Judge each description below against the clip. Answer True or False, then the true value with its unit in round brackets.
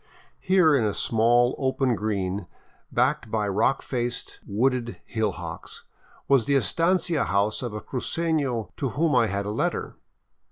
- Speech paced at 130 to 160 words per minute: True (145 wpm)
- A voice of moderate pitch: False (120 Hz)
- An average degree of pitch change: True (4.6 semitones)